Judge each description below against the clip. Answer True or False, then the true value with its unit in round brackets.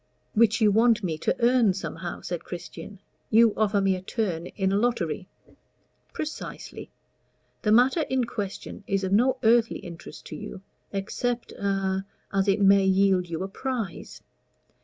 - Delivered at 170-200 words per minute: False (155 wpm)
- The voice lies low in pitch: False (200 Hz)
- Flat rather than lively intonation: False (3.4 semitones)